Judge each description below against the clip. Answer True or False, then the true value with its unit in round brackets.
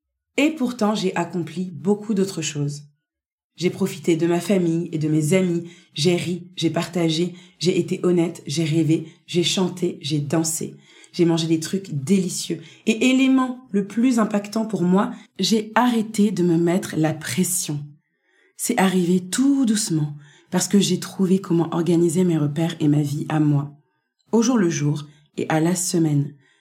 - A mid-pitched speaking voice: True (175 Hz)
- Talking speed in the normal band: True (165 wpm)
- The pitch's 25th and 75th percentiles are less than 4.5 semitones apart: True (3.5 semitones)